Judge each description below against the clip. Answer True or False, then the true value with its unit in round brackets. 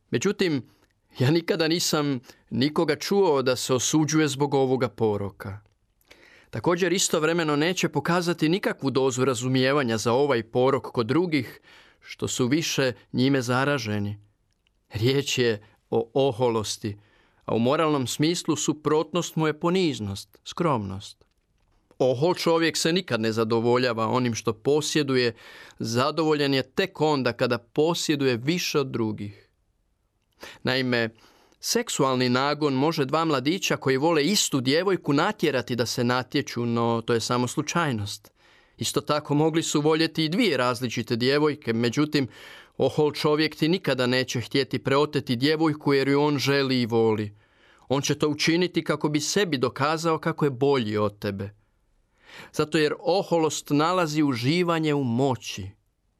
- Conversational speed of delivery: True (130 wpm)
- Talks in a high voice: False (135 Hz)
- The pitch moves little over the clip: False (5.0 semitones)